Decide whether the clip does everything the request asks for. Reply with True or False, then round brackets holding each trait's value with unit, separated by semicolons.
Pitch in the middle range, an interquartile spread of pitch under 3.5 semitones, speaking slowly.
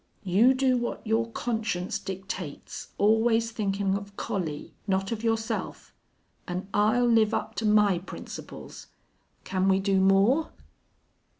False (210 Hz; 2.9 semitones; 125 wpm)